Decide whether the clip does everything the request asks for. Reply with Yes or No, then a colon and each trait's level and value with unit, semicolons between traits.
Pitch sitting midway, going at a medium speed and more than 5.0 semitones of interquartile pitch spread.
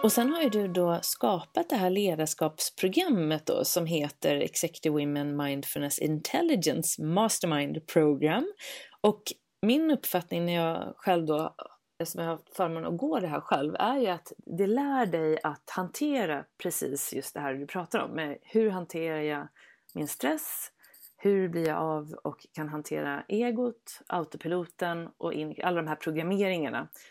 Yes: medium, 170 Hz; average, 150 wpm; wide, 5.4 semitones